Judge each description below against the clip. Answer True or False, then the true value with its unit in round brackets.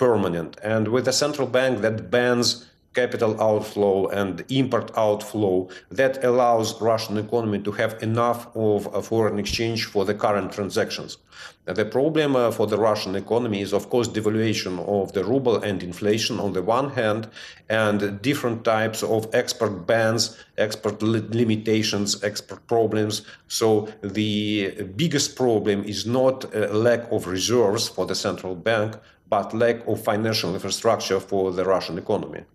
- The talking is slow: False (145 wpm)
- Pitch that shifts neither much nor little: False (2.3 semitones)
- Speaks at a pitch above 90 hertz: True (110 Hz)